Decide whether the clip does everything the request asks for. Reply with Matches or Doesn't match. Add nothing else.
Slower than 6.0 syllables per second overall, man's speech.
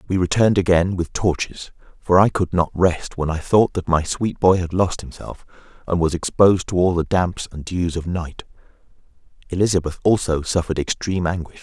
Matches